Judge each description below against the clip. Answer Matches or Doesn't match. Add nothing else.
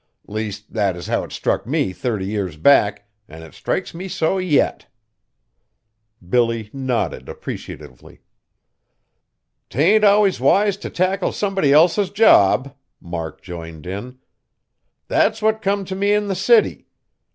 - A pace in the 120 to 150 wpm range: Matches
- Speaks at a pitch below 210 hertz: Matches